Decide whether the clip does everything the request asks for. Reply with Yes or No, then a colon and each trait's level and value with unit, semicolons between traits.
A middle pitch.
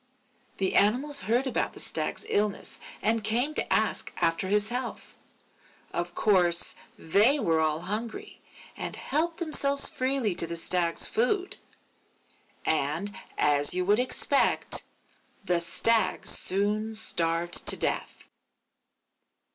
No: high, 205 Hz